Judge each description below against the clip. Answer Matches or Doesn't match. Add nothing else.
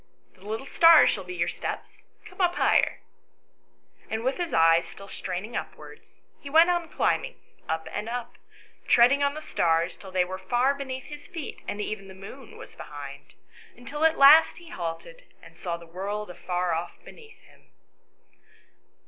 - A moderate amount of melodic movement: Doesn't match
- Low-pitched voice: Doesn't match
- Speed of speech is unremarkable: Matches